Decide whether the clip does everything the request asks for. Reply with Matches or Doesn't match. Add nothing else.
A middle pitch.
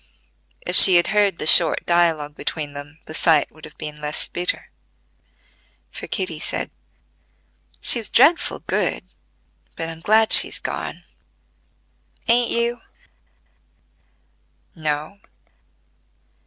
Matches